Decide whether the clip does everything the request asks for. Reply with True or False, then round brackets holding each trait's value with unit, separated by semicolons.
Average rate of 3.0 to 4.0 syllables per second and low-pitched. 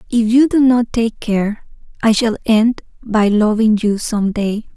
False (3.9 syllables/s; 220 Hz)